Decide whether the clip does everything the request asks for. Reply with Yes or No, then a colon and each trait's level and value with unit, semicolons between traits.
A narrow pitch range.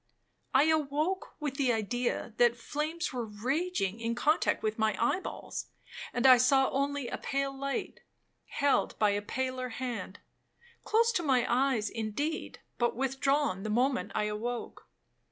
No: average, 3.8 semitones